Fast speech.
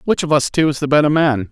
Yes: fast, 315 wpm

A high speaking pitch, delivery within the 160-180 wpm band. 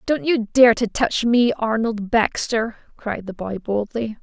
Yes: high, 225 Hz; average, 170 wpm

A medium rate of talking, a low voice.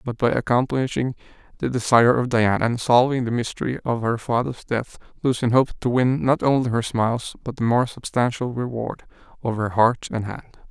Yes: average, 185 wpm; low, 120 Hz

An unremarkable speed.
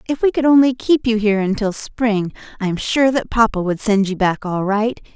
No: fast, 235 wpm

